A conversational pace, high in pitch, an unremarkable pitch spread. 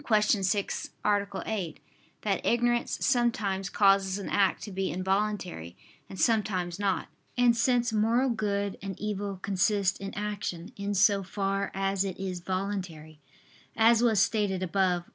No: average, 145 wpm; high, 200 Hz; narrow, 2.0 semitones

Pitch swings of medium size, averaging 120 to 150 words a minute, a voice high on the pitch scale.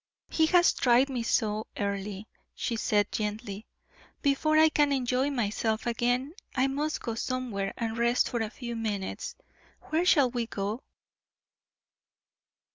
Yes: average, 4.0 semitones; slow, 135 wpm; high, 240 Hz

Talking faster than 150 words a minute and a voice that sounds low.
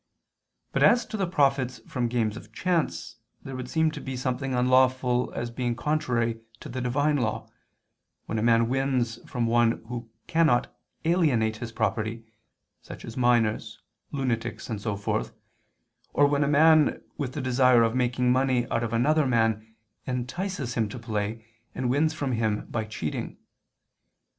Yes: average, 160 wpm; low, 125 Hz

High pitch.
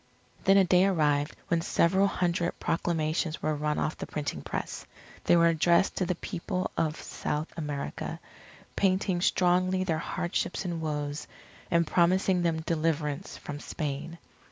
No: medium, 170 Hz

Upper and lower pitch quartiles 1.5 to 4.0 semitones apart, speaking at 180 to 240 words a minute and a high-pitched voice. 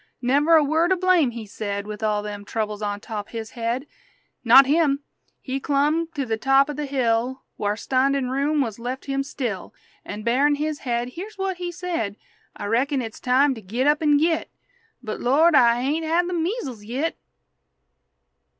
No: average, 4.8 semitones; average, 185 wpm; very high, 270 Hz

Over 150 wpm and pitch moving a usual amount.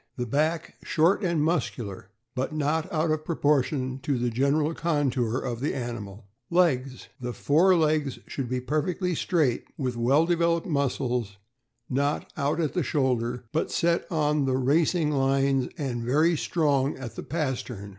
Yes: average, 165 wpm; average, 3.9 semitones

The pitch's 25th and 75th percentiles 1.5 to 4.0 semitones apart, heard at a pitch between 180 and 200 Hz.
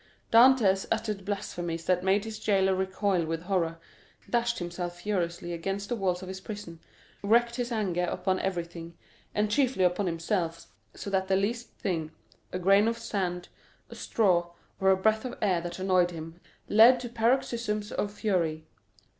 Yes: average, 3.5 semitones; high, 190 Hz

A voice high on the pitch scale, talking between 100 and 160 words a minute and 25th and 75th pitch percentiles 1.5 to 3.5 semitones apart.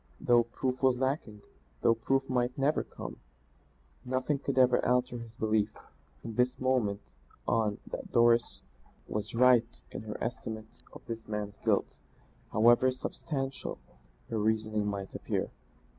No: low, 120 Hz; slow, 135 wpm; average, 2.9 semitones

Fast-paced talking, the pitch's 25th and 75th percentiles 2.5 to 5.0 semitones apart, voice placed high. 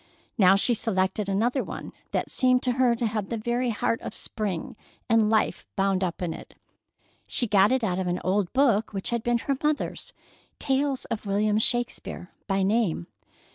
No: average, 175 wpm; average, 3.7 semitones; high, 220 Hz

